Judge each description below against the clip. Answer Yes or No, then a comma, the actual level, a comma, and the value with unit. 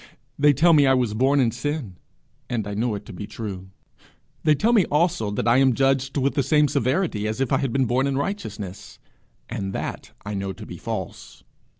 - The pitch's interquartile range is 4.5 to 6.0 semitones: Yes, average, 5.0 semitones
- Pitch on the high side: No, low, 130 Hz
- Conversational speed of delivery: No, fast, 215 wpm